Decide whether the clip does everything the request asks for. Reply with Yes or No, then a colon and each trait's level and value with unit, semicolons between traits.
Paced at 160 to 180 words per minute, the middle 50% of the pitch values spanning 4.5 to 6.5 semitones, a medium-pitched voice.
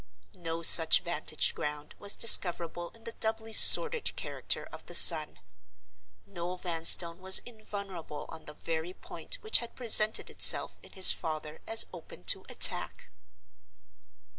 No: average, 140 wpm; average, 5.2 semitones; medium, 175 Hz